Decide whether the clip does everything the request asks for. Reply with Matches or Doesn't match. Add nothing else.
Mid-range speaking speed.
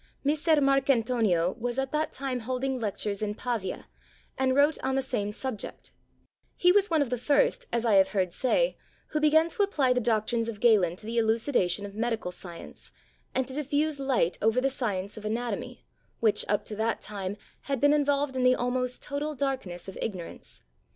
Matches